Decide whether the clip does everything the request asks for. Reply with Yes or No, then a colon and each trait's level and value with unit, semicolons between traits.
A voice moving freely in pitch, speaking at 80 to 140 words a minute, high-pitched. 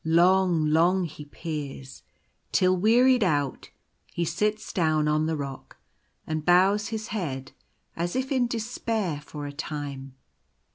No: wide, 5.8 semitones; slow, 135 wpm; medium, 170 Hz